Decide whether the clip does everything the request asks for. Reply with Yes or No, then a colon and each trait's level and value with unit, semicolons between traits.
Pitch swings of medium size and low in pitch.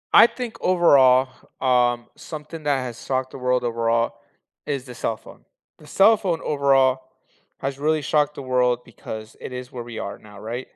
Yes: average, 3.5 semitones; low, 130 Hz